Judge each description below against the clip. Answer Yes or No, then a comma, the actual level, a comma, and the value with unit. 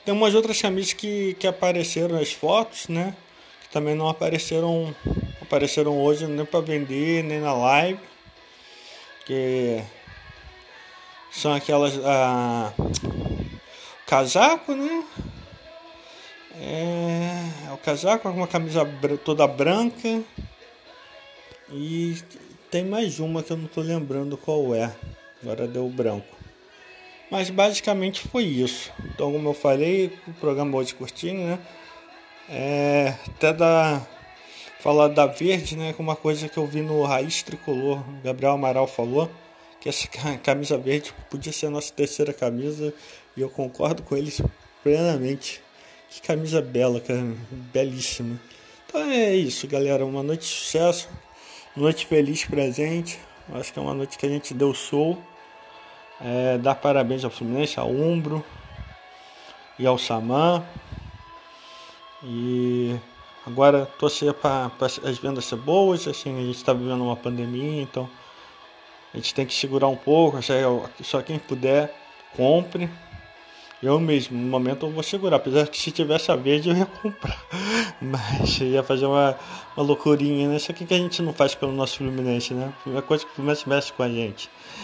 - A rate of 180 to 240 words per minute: No, average, 150 wpm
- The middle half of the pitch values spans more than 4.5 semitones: No, average, 4.0 semitones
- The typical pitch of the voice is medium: Yes, medium, 145 Hz